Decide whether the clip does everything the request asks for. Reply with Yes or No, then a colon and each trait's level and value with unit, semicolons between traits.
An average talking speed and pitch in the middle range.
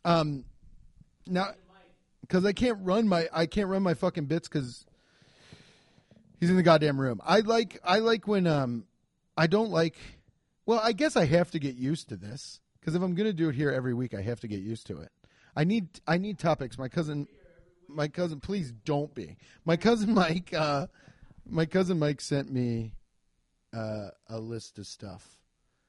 Yes: average, 185 wpm; medium, 160 Hz